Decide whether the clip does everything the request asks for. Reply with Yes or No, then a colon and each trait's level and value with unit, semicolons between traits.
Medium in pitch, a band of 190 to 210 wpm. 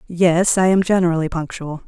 No: medium, 175 Hz; average, 160 wpm